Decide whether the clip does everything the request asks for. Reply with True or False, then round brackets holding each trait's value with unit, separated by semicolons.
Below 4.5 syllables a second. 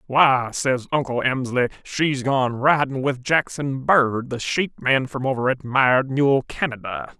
True (4.1 syllables/s)